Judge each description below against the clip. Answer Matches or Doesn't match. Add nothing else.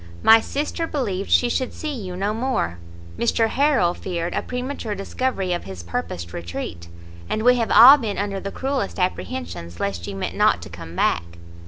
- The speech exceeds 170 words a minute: Matches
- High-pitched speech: Matches